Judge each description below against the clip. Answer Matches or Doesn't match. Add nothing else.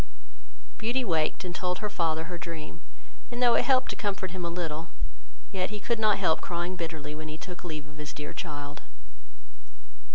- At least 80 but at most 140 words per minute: Doesn't match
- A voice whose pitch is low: Doesn't match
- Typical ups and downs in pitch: Matches